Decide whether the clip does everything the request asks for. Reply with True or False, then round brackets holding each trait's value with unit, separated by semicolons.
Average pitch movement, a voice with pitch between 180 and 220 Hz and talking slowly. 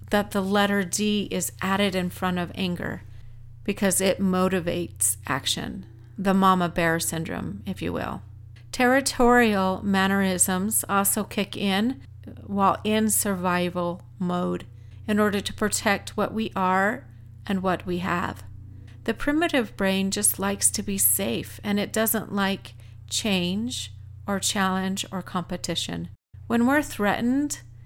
False (7.1 semitones; 190 Hz; 130 wpm)